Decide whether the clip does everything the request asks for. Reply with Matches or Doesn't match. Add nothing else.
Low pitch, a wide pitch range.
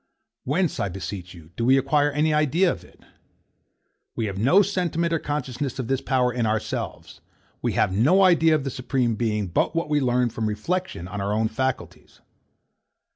Matches